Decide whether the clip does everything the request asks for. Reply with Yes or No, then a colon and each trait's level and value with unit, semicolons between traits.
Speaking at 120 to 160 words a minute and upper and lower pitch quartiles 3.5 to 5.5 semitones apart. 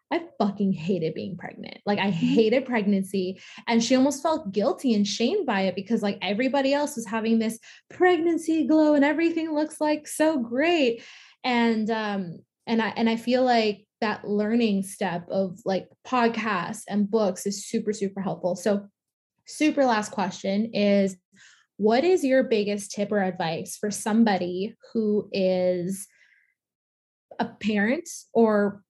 Yes: average, 150 wpm; average, 4.2 semitones